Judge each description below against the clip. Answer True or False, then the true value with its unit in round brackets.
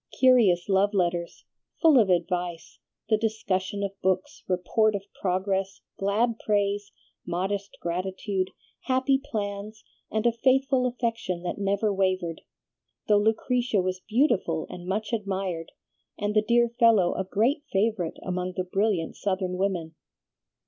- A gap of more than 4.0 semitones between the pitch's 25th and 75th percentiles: False (3.2 semitones)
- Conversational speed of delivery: False (130 wpm)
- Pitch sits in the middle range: False (200 Hz)